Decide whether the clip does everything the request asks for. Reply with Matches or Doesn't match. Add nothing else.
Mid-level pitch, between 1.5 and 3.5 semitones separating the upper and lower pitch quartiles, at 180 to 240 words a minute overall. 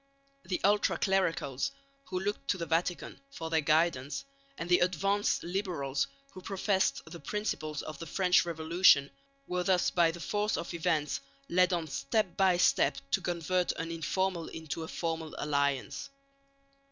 Doesn't match